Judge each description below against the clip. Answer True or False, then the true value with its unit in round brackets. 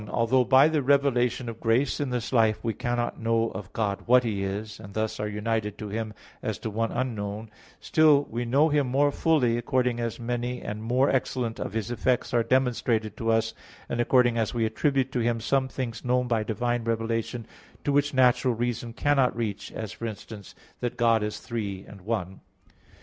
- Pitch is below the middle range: True (115 Hz)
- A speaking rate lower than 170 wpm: False (195 wpm)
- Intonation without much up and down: True (2.3 semitones)